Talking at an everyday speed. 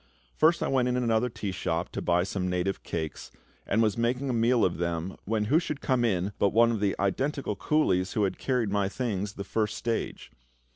No: fast, 210 wpm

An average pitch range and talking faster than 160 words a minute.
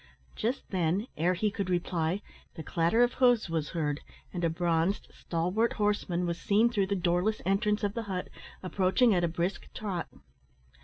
Yes: average, 3.5 semitones; average, 170 wpm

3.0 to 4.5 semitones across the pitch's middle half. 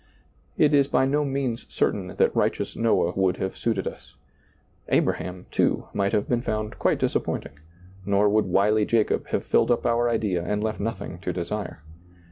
Yes: average, 3.4 semitones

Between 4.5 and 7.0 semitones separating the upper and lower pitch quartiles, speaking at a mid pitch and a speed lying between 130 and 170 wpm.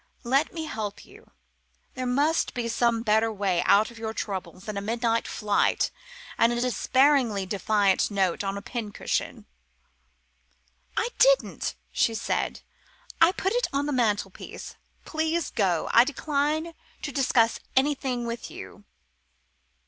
No: average, 5.3 semitones; high, 235 Hz; average, 140 wpm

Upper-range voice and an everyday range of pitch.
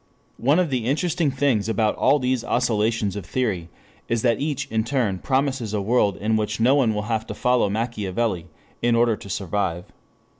No: low, 115 Hz; average, 3.6 semitones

